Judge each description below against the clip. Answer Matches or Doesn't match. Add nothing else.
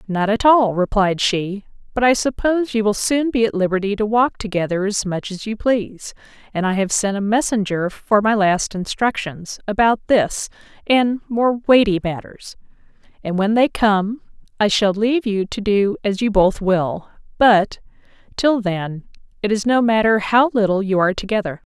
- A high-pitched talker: Matches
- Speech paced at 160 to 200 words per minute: Matches